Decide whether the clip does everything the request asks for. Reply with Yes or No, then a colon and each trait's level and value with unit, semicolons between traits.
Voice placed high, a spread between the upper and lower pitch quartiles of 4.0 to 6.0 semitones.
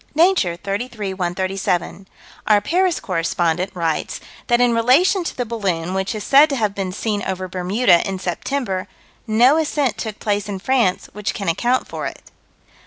Yes: high, 205 Hz; average, 4.9 semitones